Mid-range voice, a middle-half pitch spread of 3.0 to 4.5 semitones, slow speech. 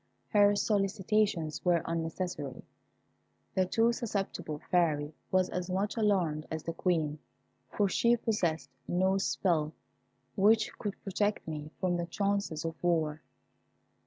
Yes: medium, 180 Hz; average, 4.0 semitones; slow, 125 wpm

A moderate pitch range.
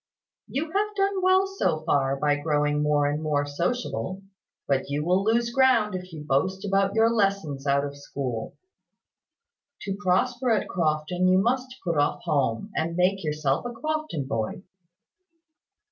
No: wide, 7.9 semitones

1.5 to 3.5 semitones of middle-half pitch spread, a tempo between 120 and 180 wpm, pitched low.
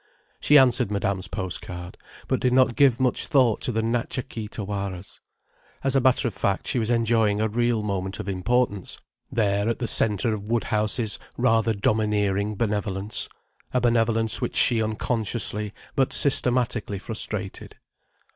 Yes: average, 2.8 semitones; average, 150 wpm; low, 110 Hz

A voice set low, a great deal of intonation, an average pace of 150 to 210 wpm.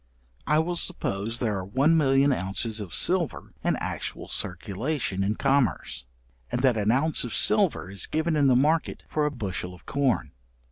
Yes: low, 130 Hz; wide, 7.1 semitones; average, 175 wpm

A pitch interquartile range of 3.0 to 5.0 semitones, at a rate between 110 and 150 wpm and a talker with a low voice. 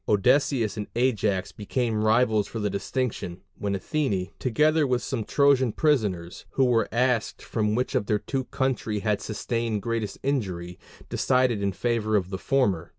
No: average, 3.9 semitones; average, 160 wpm; low, 110 Hz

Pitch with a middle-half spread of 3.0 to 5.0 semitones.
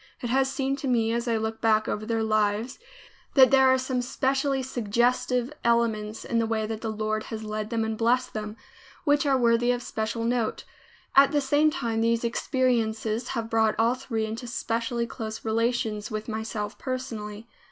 No: narrow, 2.6 semitones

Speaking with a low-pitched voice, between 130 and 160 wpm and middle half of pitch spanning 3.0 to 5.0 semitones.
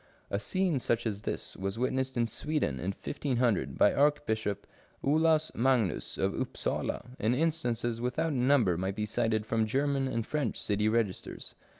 Yes: low, 120 Hz; average, 155 wpm; average, 4.7 semitones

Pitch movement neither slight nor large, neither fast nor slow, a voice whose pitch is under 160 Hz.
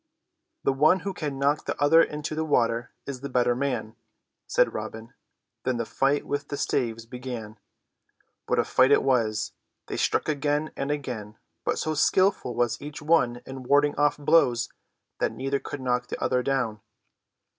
Yes: average, 3.2 semitones; average, 170 wpm; low, 135 Hz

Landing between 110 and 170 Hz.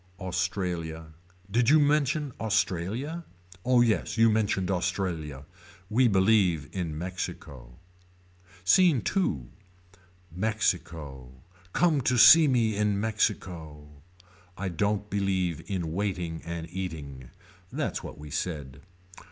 No: very low, 95 Hz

